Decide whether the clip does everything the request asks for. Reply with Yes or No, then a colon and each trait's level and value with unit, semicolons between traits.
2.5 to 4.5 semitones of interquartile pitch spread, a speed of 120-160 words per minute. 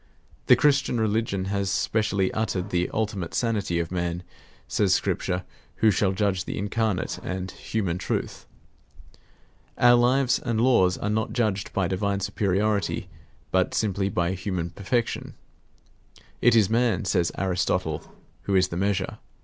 Yes: average, 3.1 semitones; average, 140 wpm